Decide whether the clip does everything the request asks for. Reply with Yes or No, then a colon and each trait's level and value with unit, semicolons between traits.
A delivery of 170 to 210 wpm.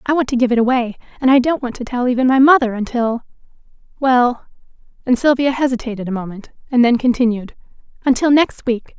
Yes: average, 180 wpm